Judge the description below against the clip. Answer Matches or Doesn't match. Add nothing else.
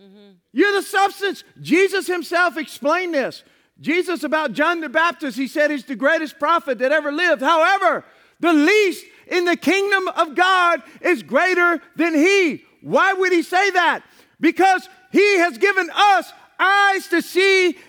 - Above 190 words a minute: Doesn't match